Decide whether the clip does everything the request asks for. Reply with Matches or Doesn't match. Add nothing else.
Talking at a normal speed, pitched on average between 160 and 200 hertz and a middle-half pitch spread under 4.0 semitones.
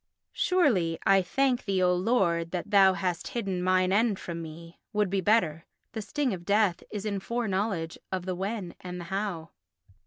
Matches